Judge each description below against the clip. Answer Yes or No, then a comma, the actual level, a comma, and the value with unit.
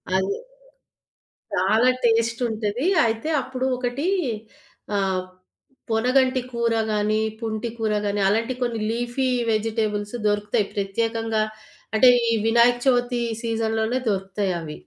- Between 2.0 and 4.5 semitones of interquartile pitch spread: Yes, narrow, 2.5 semitones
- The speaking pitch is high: Yes, high, 225 Hz